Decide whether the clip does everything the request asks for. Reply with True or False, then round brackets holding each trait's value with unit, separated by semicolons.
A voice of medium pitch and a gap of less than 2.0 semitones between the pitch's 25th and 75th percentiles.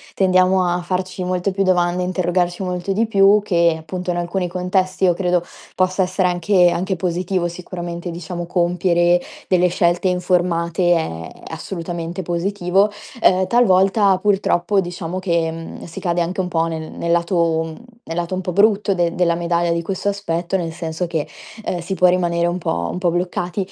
True (180 Hz; 1.5 semitones)